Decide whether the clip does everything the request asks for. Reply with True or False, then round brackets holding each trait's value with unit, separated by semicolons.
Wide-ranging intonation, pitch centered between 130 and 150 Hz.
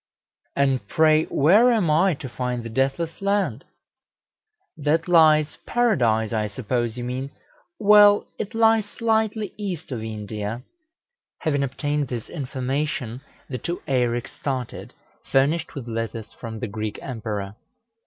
True (6.2 semitones; 135 Hz)